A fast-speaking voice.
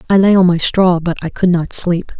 Yes: fast, 275 wpm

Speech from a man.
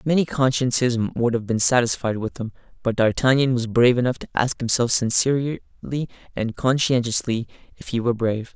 Yes: male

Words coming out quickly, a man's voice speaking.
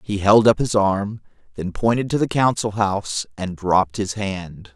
No: average, 190 wpm; male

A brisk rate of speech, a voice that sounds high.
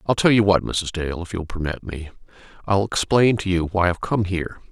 No: fast, 240 wpm; very low, 95 Hz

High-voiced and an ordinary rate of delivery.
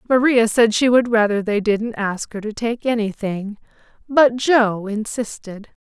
Yes: high, 220 Hz; average, 155 wpm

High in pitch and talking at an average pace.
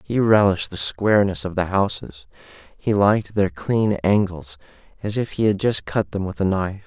No: very low, 95 Hz; average, 190 wpm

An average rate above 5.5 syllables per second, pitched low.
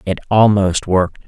No: 5.1 syllables/s; very low, 95 Hz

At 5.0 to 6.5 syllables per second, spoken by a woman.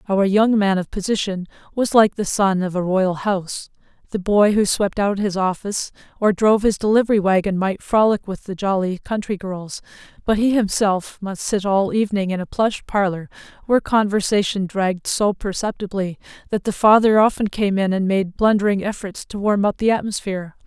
Yes: 5.3 syllables/s; female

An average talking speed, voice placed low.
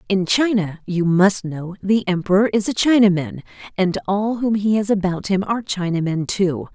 No: average, 180 wpm; high, 195 Hz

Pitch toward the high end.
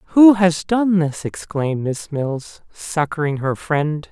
No: medium, 165 Hz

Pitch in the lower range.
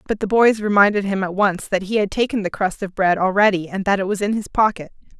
No: high, 200 Hz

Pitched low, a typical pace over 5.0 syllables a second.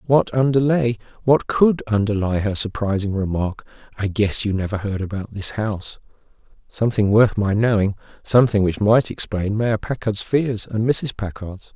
No: low, 110 Hz; 4.8 syllables/s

